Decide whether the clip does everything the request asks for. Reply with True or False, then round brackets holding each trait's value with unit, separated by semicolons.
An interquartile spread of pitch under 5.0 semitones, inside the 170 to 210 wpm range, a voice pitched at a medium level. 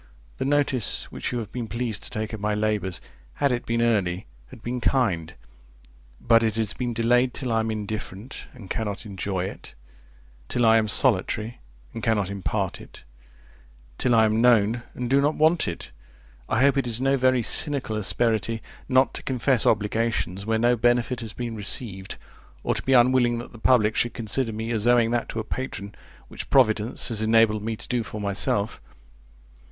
False (2.4 semitones; 185 wpm; 115 Hz)